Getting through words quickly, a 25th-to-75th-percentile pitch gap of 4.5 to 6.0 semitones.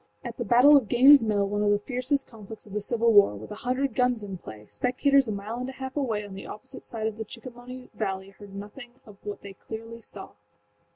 No: fast, 235 wpm; average, 3.6 semitones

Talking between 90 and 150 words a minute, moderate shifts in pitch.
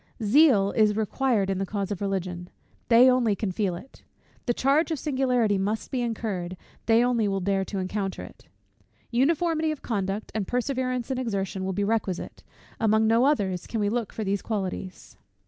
No: average, 180 wpm; average, 4.2 semitones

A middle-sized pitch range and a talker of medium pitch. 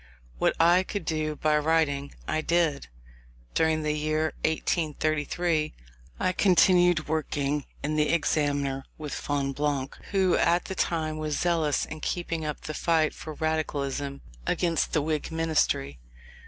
No: narrow, 1.9 semitones; medium, 155 Hz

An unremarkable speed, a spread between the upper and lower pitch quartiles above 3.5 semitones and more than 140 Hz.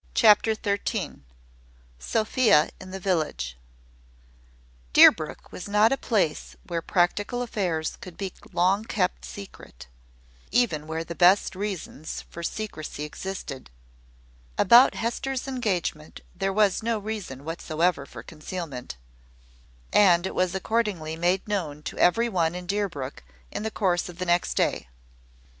No: slow, 130 wpm; average, 4.5 semitones; medium, 185 Hz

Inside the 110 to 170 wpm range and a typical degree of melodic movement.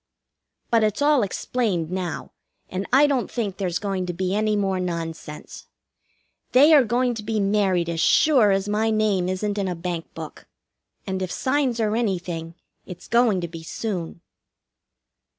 Yes: average, 165 wpm; average, 3.9 semitones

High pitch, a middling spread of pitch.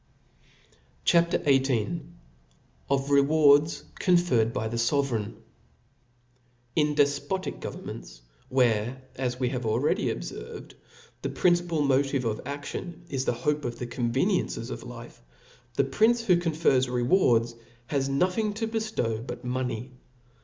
No: low, 135 Hz; average, 4.8 semitones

